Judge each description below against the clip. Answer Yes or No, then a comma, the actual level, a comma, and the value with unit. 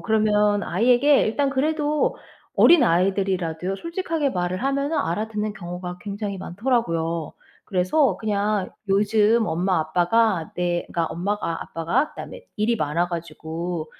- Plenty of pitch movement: No, average, 4.8 semitones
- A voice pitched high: Yes, high, 200 Hz